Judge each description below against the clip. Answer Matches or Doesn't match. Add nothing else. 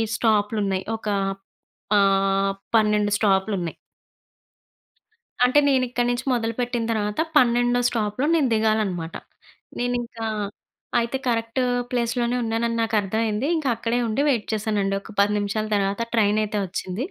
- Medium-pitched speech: Doesn't match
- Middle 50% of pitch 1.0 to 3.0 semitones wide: Matches